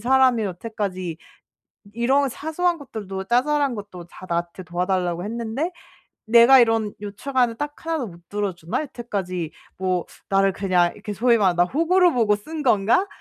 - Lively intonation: Yes, wide, 5.9 semitones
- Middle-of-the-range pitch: No, high, 215 Hz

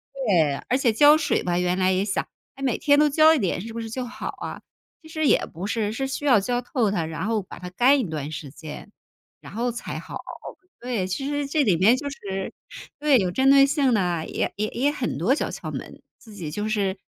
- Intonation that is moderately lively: No, wide, 6.6 semitones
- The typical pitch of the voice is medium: No, high, 225 Hz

